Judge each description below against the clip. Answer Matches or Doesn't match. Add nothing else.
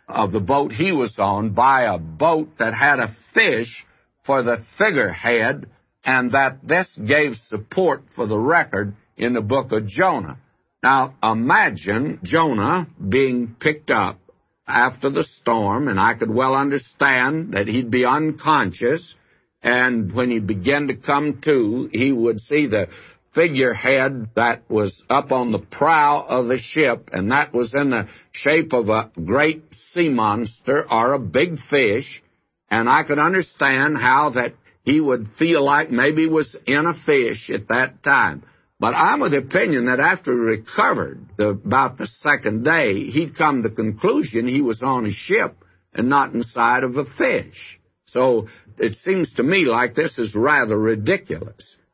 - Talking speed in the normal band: Matches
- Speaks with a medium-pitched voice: Doesn't match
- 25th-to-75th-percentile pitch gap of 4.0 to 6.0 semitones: Matches